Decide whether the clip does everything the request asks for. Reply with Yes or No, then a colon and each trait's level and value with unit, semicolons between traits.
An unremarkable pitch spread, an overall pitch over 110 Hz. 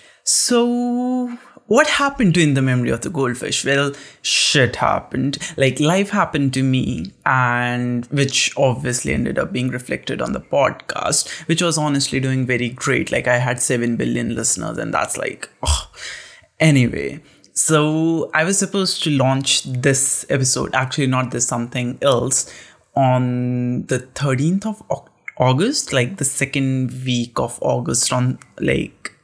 Yes: average, 4.0 semitones; low, 135 Hz